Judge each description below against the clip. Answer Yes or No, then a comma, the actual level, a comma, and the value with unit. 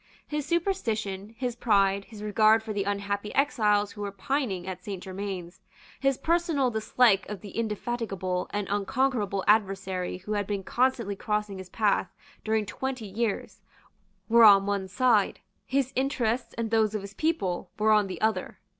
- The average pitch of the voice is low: No, high, 210 Hz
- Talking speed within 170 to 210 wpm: No, average, 160 wpm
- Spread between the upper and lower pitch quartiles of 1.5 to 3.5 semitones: Yes, average, 3.2 semitones